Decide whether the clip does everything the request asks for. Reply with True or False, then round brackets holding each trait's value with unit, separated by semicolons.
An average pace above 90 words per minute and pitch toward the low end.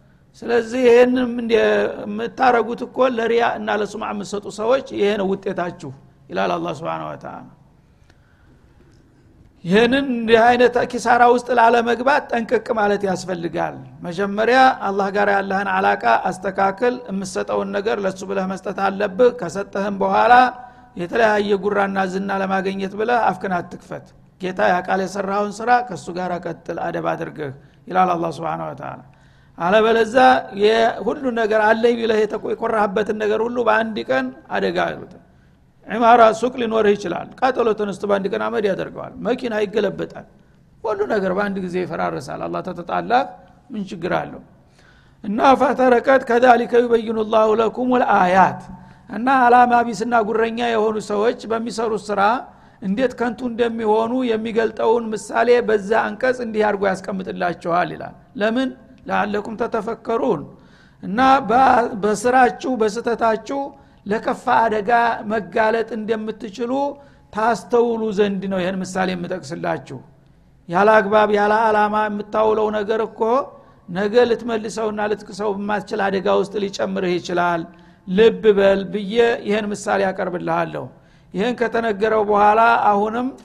False (110 wpm; 215 Hz)